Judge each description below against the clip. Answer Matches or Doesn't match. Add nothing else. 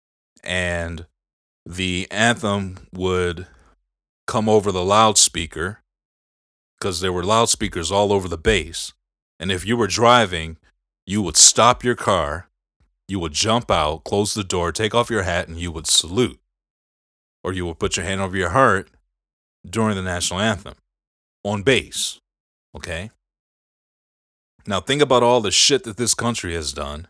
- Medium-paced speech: Matches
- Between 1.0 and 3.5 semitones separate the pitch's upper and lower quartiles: Doesn't match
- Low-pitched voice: Matches